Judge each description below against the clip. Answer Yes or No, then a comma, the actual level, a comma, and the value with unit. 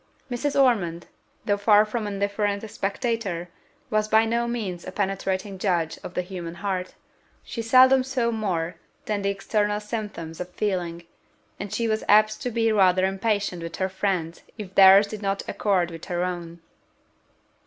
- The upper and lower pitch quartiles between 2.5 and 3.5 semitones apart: Yes, average, 3.0 semitones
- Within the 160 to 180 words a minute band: Yes, average, 165 wpm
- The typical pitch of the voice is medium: No, high, 200 Hz